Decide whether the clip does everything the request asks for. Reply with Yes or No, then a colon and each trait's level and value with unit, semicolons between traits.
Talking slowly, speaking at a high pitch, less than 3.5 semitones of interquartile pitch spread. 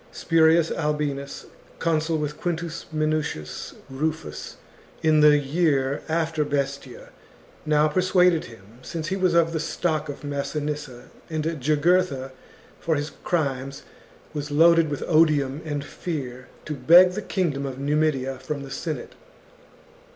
No: slow, 130 wpm; medium, 150 Hz; average, 2.8 semitones